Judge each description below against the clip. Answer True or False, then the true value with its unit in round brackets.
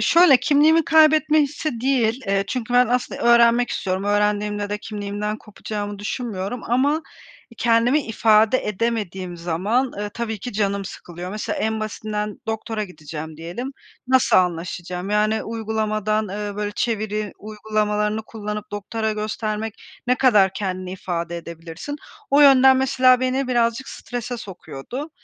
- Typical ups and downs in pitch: True (3.3 semitones)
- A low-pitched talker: False (215 Hz)